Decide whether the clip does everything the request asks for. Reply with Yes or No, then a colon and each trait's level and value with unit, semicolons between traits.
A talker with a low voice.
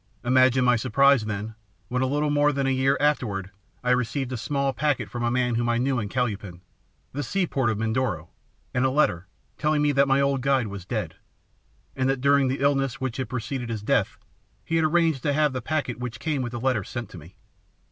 Yes: low, 130 Hz